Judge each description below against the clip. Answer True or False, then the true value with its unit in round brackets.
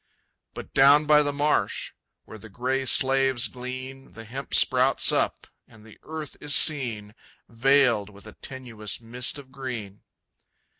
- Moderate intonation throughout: True (3.4 semitones)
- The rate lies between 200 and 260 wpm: False (145 wpm)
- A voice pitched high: False (130 Hz)